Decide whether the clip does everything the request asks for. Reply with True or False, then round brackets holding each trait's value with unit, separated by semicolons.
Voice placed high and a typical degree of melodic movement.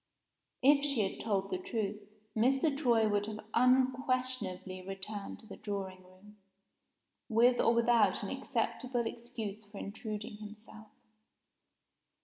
True (220 Hz; 3.5 semitones)